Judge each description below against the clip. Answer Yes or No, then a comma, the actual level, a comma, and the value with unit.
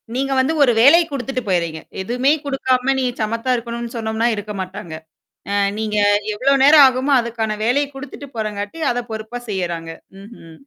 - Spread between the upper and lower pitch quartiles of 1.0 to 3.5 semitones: No, average, 4.1 semitones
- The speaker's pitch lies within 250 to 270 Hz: No, high, 235 Hz